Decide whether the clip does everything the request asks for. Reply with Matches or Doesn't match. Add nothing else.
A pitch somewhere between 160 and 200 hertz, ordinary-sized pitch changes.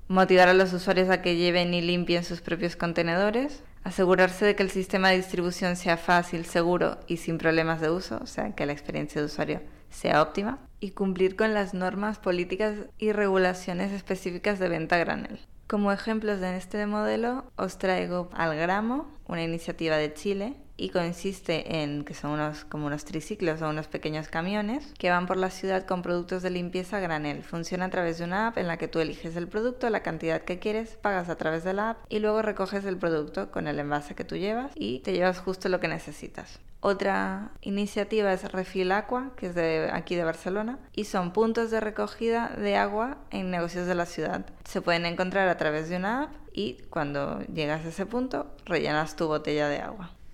Matches